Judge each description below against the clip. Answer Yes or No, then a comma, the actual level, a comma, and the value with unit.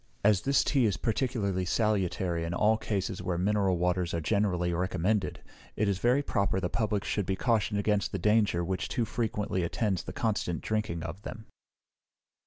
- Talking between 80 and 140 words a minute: No, average, 175 wpm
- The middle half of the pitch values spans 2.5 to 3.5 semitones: Yes, average, 3.2 semitones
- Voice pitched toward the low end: Yes, low, 100 Hz